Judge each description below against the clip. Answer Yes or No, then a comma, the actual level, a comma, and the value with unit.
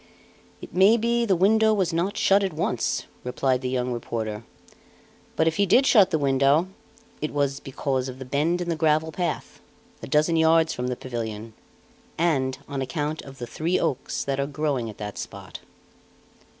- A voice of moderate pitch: Yes, medium, 150 Hz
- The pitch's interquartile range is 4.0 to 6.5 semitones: Yes, average, 4.8 semitones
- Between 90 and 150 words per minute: No, average, 180 wpm